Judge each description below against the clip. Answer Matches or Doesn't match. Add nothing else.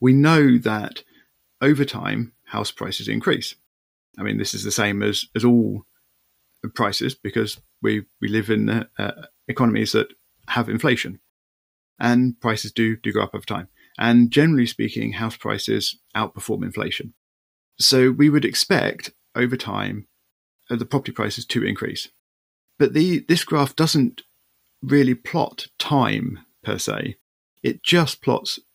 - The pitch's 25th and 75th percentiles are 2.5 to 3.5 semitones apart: Doesn't match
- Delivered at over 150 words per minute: Doesn't match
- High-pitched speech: Doesn't match